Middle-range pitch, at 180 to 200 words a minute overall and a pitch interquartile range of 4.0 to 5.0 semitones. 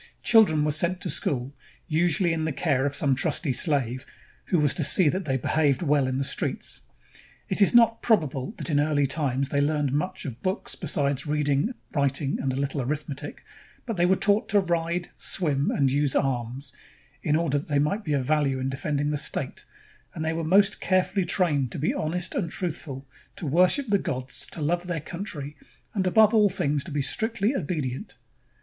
Yes: medium, 150 Hz; average, 195 wpm; average, 4.3 semitones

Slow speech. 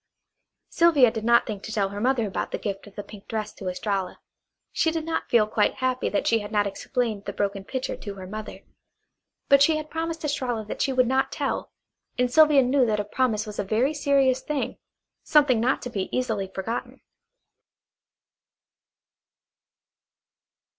No: average, 175 wpm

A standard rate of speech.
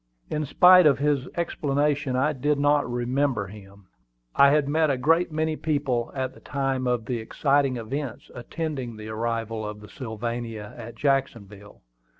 Yes: average, 155 wpm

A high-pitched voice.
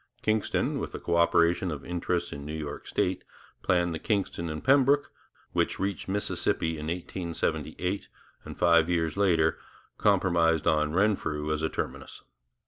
No: very low, 85 Hz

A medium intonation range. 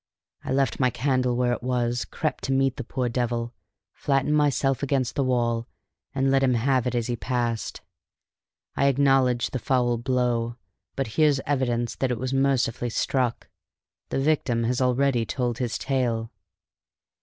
No: narrow, 2.0 semitones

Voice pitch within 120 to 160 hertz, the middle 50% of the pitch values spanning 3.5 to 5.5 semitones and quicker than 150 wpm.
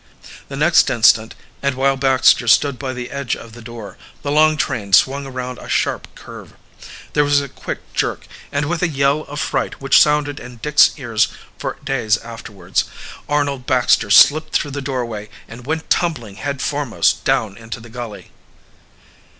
Yes: low, 135 Hz; average, 3.8 semitones; average, 170 wpm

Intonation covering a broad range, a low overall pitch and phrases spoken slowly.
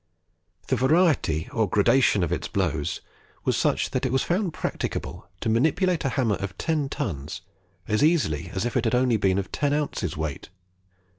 No: wide, 7.5 semitones; low, 115 Hz; average, 175 wpm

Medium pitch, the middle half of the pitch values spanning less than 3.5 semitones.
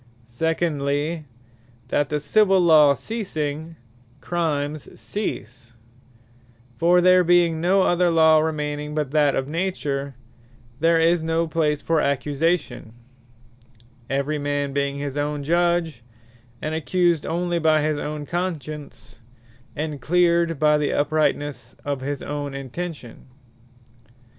Yes: medium, 155 Hz; average, 2.9 semitones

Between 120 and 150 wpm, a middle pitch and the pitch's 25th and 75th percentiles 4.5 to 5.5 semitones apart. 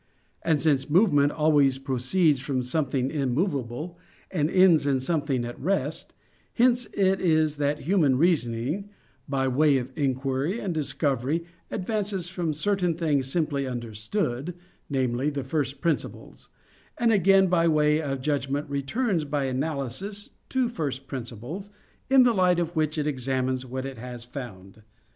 Yes: average, 140 wpm; medium, 145 Hz; average, 4.8 semitones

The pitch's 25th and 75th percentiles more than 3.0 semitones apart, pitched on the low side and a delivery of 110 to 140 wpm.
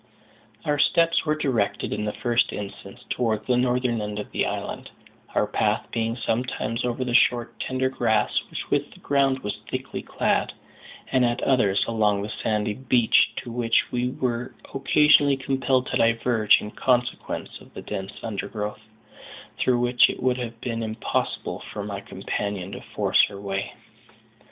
No: average, 3.4 semitones; low, 120 Hz; average, 160 wpm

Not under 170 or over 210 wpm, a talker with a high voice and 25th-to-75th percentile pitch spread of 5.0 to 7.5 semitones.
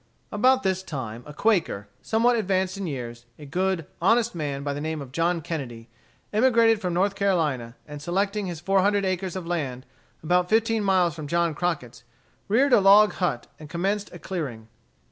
No: average, 180 wpm; medium, 180 Hz; average, 5.3 semitones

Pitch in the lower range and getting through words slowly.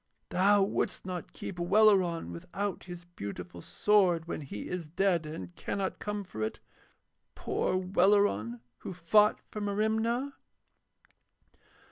No: medium, 185 Hz; slow, 120 wpm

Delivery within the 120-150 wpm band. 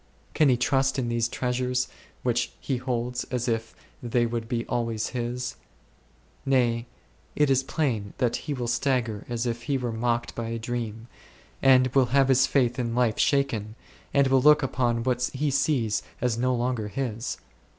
No: average, 170 wpm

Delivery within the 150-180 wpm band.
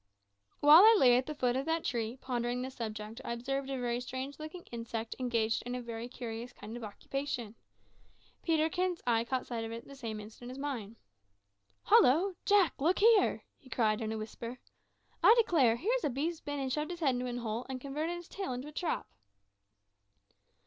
No: average, 195 wpm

